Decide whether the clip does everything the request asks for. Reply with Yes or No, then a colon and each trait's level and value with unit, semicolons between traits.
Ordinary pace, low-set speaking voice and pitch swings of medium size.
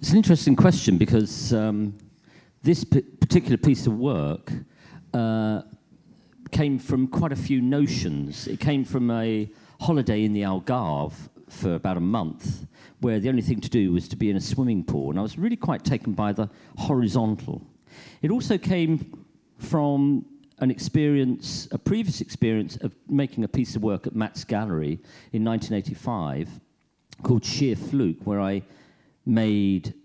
Yes: average, 160 wpm; low, 120 Hz; average, 4.9 semitones